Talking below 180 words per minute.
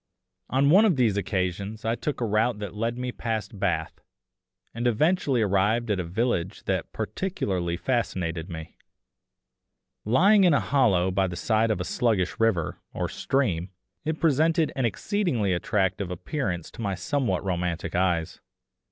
Yes: average, 150 wpm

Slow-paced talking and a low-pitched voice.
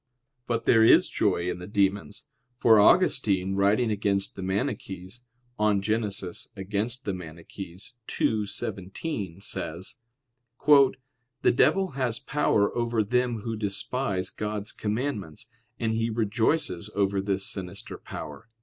Yes: slow, 120 wpm; low, 105 Hz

